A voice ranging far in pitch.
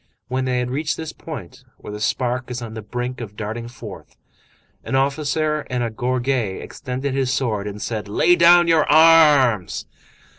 No: average, 4.3 semitones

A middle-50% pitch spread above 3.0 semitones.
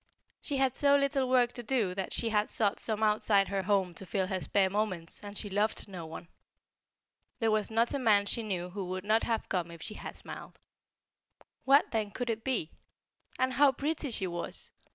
Yes: average, 4.2 semitones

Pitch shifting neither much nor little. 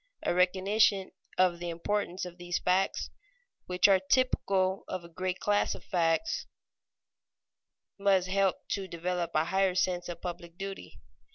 No: narrow, 1.7 semitones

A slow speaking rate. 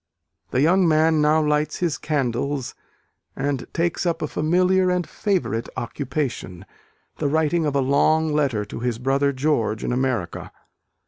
No: average, 145 wpm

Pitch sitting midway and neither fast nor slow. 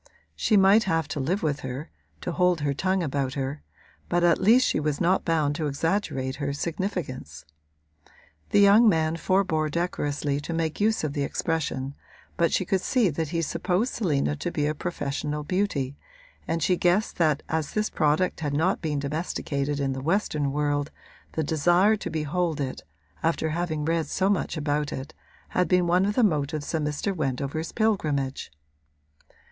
Yes: medium, 160 Hz; average, 175 wpm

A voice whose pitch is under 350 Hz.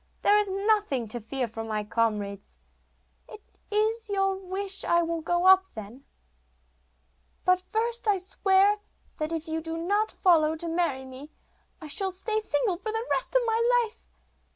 No: very high, 365 Hz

